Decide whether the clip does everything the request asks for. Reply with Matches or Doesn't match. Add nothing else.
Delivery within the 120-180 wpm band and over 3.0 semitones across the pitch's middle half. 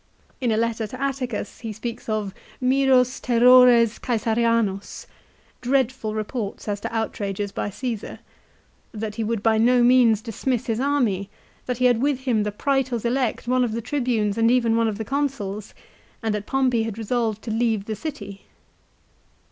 Doesn't match